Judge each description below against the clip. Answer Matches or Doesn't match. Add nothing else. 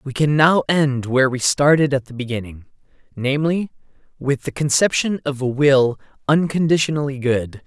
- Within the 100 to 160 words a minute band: Matches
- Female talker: Doesn't match